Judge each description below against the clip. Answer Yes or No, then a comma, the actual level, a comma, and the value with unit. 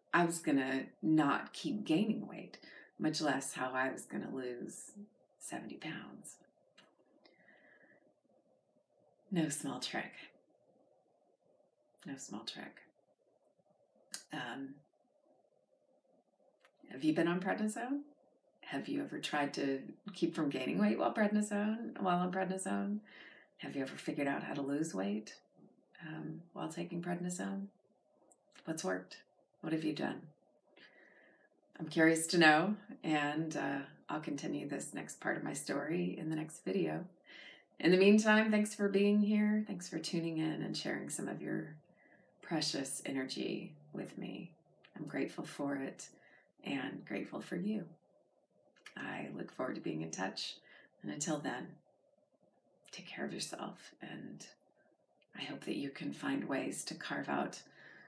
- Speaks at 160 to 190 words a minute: No, slow, 135 wpm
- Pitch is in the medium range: Yes, medium, 170 Hz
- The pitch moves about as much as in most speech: No, wide, 5.8 semitones